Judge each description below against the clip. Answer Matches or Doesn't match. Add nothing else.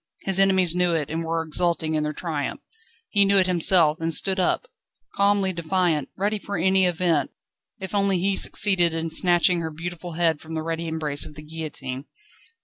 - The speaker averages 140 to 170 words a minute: Doesn't match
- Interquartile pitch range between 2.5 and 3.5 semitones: Matches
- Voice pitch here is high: Doesn't match